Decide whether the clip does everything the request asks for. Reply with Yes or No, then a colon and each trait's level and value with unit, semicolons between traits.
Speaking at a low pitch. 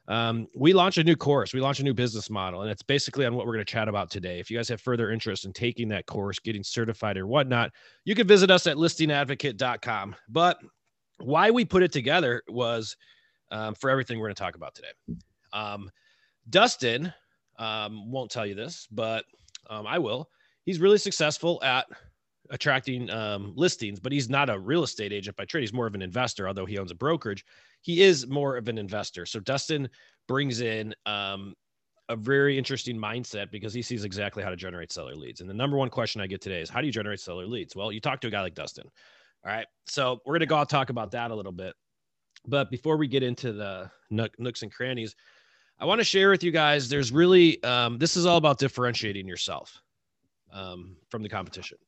Yes: low, 120 Hz